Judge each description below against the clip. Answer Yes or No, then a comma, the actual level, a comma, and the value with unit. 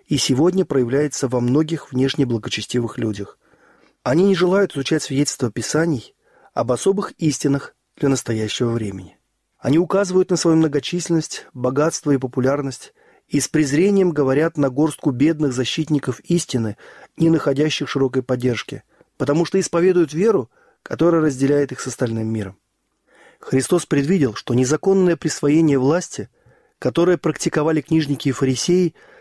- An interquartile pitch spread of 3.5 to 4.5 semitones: Yes, average, 4.1 semitones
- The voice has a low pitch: No, medium, 145 Hz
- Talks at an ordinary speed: Yes, average, 125 wpm